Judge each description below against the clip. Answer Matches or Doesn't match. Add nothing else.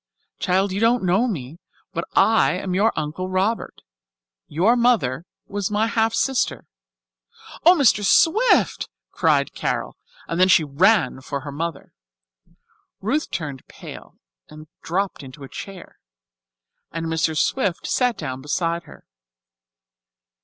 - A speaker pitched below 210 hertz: Matches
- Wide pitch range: Matches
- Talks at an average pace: Doesn't match